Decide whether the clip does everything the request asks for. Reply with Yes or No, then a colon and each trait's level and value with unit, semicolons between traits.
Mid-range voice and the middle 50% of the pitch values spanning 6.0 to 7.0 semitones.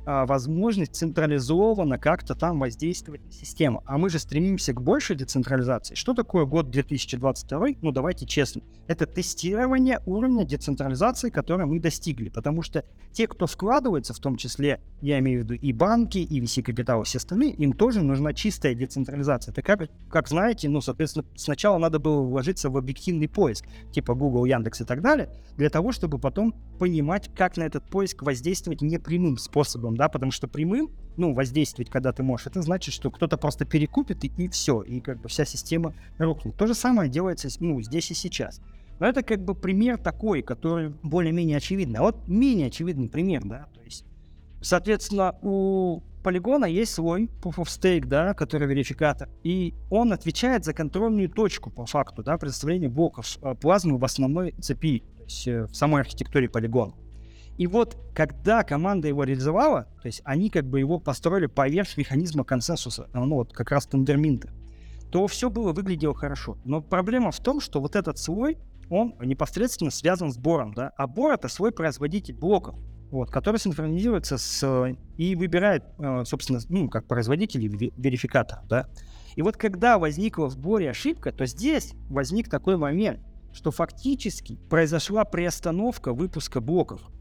No: medium, 155 Hz; wide, 5.6 semitones